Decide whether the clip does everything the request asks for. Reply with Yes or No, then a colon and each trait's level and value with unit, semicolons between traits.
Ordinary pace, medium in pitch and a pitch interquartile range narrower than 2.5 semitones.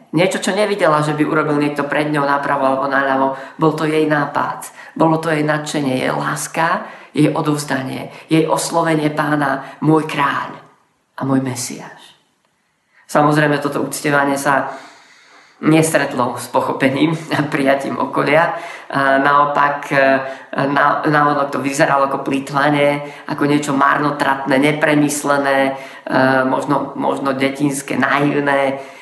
Yes: average, 120 wpm; medium, 145 Hz; narrow, 1.8 semitones